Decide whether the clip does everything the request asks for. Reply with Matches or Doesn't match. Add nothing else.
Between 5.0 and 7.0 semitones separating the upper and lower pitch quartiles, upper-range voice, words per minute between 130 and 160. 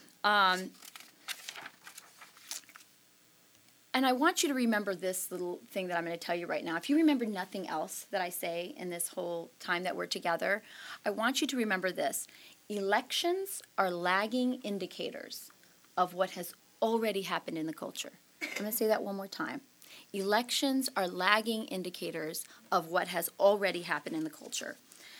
Doesn't match